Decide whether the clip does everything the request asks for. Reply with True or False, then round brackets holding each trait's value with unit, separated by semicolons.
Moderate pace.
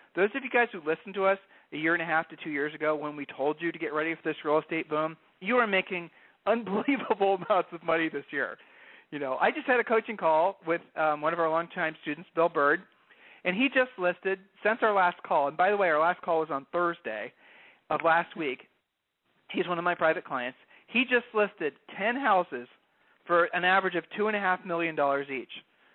False (225 wpm)